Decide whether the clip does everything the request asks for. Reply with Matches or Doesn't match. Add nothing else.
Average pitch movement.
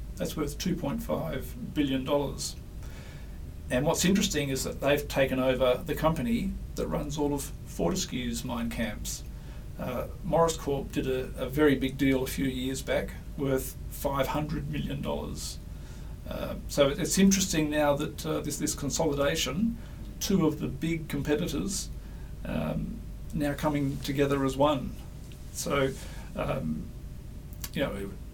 Matches